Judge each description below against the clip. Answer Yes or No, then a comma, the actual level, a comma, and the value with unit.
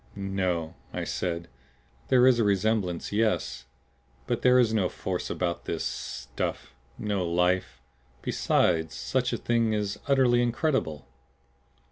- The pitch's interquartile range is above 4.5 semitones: Yes, average, 5.3 semitones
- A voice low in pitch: Yes, very low, 95 Hz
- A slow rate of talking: Yes, slow, 125 wpm